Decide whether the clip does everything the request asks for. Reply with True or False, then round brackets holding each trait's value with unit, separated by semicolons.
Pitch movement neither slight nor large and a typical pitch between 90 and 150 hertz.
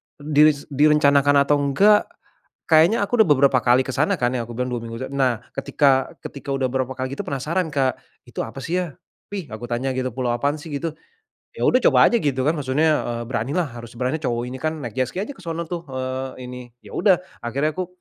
True (3.6 semitones; 140 Hz)